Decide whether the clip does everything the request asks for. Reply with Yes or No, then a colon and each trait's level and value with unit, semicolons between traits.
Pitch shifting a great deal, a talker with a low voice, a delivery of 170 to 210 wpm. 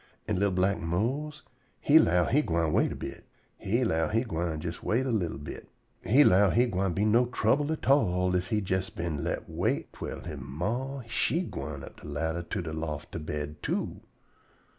Yes: wide, 6.5 semitones; very low, 95 Hz; average, 200 wpm